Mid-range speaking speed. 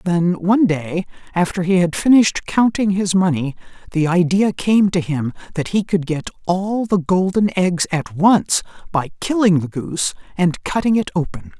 Yes: average, 170 wpm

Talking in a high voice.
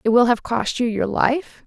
Yes: high, 245 Hz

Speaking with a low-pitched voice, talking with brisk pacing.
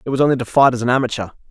Yes: low, 125 Hz; fast, 320 wpm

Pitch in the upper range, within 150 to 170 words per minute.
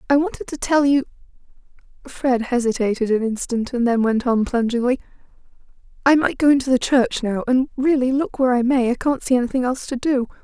No: very high, 255 Hz; average, 195 wpm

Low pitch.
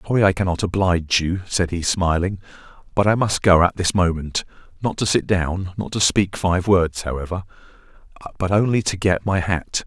Yes: very low, 90 Hz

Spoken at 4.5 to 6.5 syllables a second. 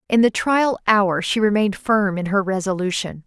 Yes: 5.0 syllables/s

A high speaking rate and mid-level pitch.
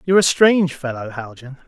No: average, 180 wpm; medium, 150 Hz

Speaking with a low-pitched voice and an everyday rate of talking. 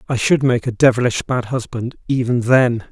Yes: low, 120 Hz; average, 185 wpm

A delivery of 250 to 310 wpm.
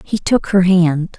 No: fast, 205 wpm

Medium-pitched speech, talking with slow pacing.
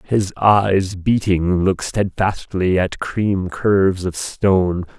No: very low, 95 Hz; slow, 120 wpm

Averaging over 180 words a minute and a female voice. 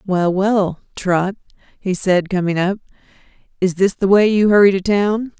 No: average, 165 wpm; female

